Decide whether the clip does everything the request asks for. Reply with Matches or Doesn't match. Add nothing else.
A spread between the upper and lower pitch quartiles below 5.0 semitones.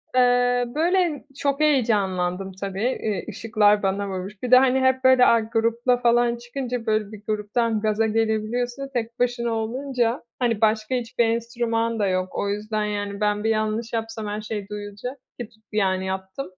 Matches